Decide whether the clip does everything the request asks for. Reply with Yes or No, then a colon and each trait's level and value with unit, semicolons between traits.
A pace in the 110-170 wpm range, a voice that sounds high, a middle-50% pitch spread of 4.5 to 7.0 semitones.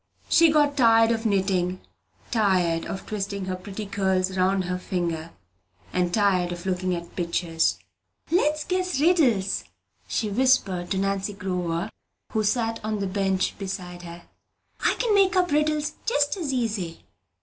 Yes: average, 150 wpm; high, 195 Hz; wide, 5.5 semitones